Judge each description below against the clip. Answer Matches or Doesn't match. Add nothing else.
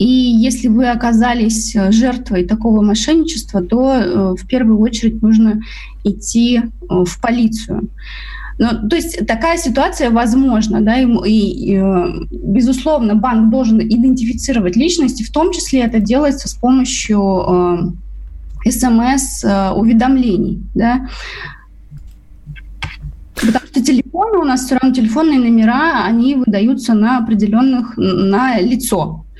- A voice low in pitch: Doesn't match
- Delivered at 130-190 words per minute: Doesn't match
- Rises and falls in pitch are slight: Doesn't match